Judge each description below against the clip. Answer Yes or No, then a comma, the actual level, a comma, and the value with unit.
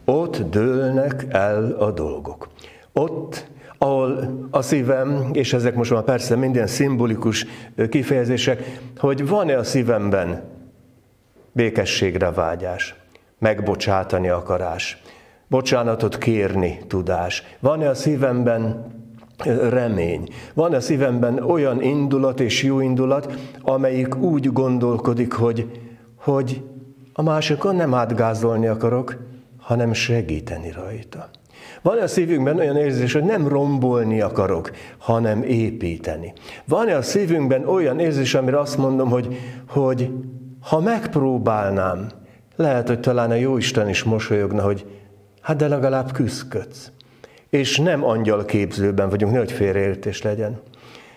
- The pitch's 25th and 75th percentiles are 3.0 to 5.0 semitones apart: Yes, average, 3.4 semitones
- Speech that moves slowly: No, average, 115 wpm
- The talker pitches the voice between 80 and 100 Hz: No, low, 125 Hz